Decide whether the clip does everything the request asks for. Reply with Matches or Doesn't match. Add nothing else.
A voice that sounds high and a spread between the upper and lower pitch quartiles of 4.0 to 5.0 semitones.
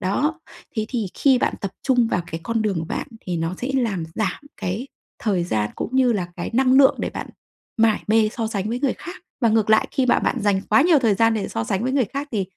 Matches